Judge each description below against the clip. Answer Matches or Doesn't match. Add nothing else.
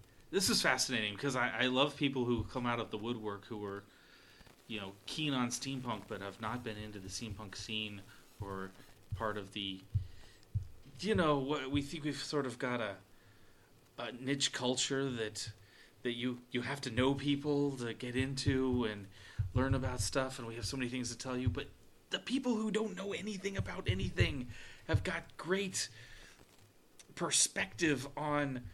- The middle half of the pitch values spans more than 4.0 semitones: Matches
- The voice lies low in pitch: Matches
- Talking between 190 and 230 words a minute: Doesn't match